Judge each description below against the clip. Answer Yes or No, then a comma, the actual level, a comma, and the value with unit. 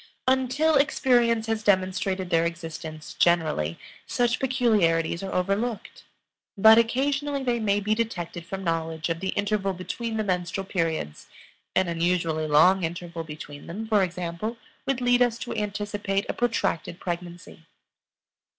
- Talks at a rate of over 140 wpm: No, slow, 135 wpm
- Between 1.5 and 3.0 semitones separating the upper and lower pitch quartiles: No, average, 5.3 semitones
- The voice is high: Yes, high, 195 Hz